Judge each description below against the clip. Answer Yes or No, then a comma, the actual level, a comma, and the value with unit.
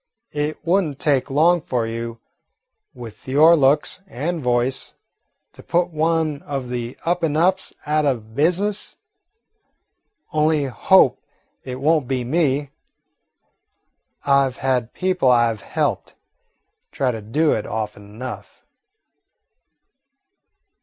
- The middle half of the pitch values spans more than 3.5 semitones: Yes, average, 4.6 semitones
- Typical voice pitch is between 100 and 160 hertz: Yes, medium, 140 Hz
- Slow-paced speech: Yes, slow, 125 wpm